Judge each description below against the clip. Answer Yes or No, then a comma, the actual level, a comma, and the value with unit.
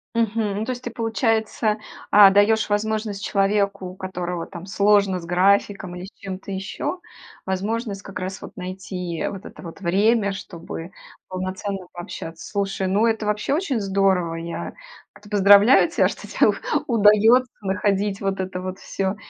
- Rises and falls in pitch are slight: Yes, narrow, 2.1 semitones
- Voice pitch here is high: Yes, high, 200 Hz